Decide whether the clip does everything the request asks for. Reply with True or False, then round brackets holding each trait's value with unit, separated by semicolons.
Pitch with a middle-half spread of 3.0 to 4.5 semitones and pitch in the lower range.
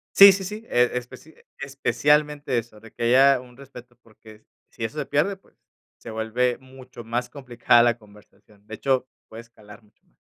True (3.4 semitones; 125 Hz)